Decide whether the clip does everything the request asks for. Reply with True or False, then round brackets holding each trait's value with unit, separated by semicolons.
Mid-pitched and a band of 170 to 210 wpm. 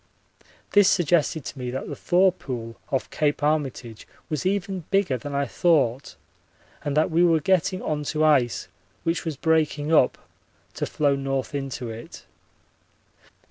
False (150 Hz; 150 wpm)